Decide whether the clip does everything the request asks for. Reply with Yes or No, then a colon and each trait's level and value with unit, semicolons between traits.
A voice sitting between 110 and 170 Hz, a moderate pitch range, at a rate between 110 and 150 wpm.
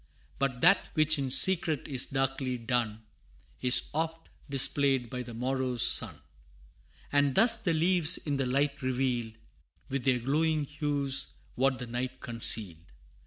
Yes: low, 135 Hz; average, 3.0 semitones; average, 140 wpm